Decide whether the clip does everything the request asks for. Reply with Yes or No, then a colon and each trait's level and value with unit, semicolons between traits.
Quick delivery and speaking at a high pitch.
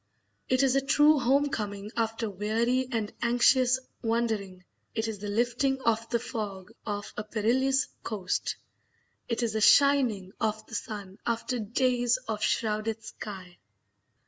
No: average, 145 wpm; high, 225 Hz